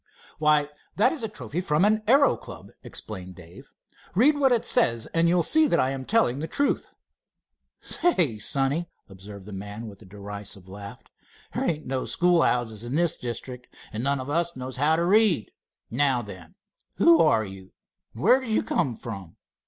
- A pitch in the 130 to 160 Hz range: Yes, low, 135 Hz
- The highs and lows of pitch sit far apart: Yes, wide, 8.4 semitones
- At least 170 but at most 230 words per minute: Yes, average, 180 wpm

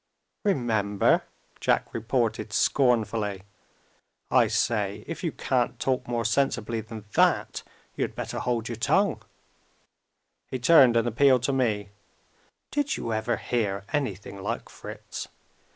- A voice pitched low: Yes, low, 115 Hz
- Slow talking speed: Yes, slow, 125 wpm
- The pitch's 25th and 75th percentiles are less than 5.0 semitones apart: Yes, average, 3.5 semitones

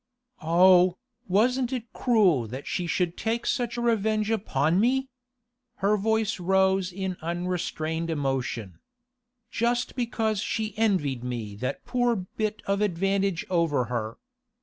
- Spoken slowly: Yes, slow, 125 wpm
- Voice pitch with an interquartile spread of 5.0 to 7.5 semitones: Yes, wide, 5.4 semitones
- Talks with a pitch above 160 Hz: Yes, high, 190 Hz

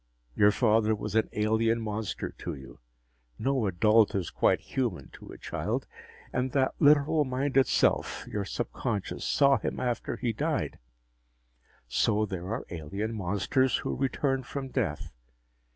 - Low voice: Yes, low, 110 Hz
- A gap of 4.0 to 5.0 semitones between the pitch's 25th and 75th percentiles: Yes, average, 4.3 semitones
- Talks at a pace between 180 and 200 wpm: No, average, 140 wpm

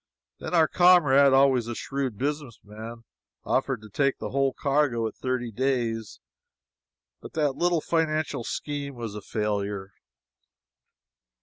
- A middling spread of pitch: Yes, average, 4.2 semitones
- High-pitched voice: No, low, 130 Hz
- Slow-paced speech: Yes, slow, 125 wpm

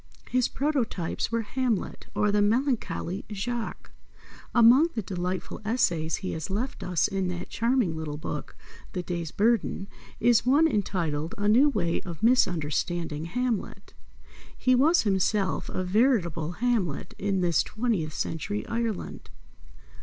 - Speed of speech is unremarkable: No, slow, 130 wpm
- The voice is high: Yes, high, 205 Hz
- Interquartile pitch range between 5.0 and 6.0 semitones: Yes, wide, 5.6 semitones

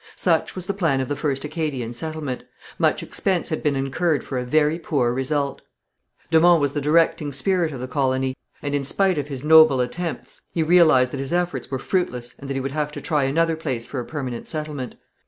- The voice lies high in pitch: No, medium, 145 Hz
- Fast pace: Yes, fast, 215 wpm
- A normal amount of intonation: Yes, average, 3.4 semitones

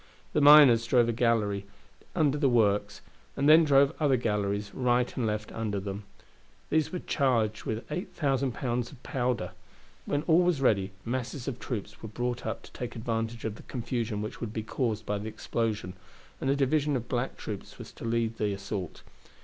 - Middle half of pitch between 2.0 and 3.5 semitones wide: No, average, 4.0 semitones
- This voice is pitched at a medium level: No, low, 115 Hz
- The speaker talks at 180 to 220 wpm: Yes, average, 190 wpm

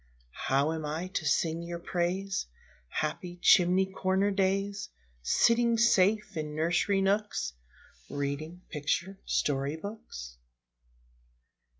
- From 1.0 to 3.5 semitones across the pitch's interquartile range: No, average, 4.0 semitones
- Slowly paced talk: Yes, slow, 100 wpm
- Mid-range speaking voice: Yes, medium, 180 Hz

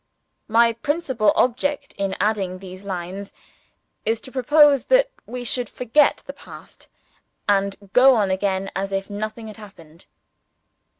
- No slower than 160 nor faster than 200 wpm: No, slow, 135 wpm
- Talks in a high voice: Yes, high, 215 Hz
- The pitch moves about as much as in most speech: Yes, average, 4.4 semitones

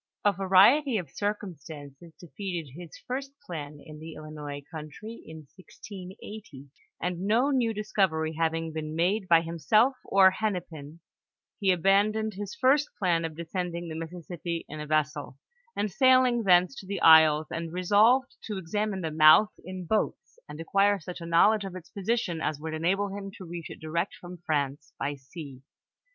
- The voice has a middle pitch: Yes, medium, 175 Hz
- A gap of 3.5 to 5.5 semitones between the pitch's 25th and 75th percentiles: Yes, average, 4.3 semitones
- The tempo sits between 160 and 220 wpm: Yes, average, 165 wpm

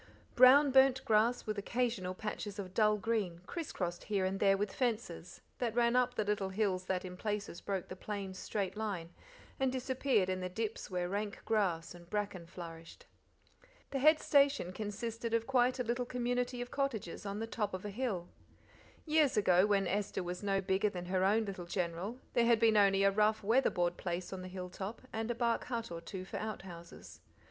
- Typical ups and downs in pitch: Yes, average, 4.2 semitones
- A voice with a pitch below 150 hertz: No, high, 205 Hz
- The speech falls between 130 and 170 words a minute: No, average, 200 wpm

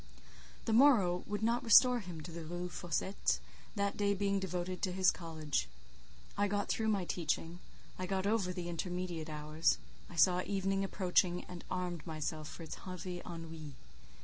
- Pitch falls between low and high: Yes, medium, 180 Hz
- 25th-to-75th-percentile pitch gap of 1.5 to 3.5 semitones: Yes, average, 2.9 semitones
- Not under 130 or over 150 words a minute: No, average, 170 wpm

